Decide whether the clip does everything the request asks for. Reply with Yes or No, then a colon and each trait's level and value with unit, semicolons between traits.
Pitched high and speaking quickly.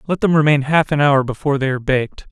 No: medium, 145 Hz; fast, 260 wpm